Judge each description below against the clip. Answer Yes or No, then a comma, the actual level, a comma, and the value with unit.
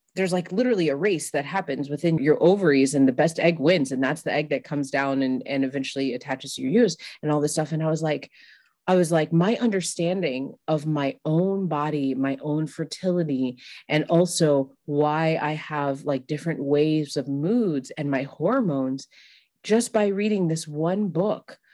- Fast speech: No, average, 190 wpm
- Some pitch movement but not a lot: Yes, average, 4.0 semitones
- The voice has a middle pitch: Yes, medium, 150 Hz